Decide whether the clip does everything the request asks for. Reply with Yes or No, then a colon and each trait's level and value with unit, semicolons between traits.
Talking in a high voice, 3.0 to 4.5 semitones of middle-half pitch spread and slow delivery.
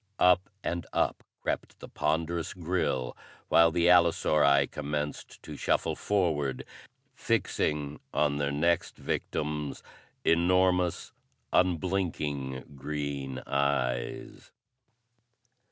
No: very low, 75 Hz; average, 3.4 semitones; slow, 90 wpm